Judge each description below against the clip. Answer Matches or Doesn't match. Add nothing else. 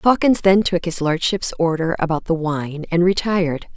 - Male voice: Doesn't match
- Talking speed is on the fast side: Doesn't match